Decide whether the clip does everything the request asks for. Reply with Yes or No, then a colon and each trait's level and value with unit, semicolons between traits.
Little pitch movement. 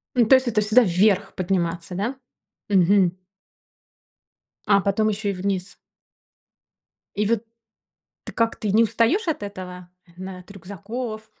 No: average, 3.1 semitones